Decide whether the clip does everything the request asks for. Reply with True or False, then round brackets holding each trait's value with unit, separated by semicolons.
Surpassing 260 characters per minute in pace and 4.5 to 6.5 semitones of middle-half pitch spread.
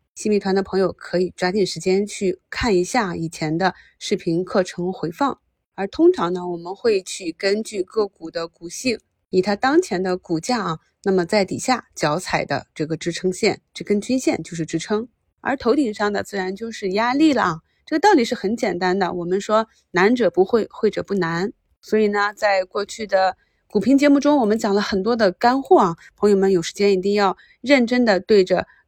False (285 characters per minute; 3.8 semitones)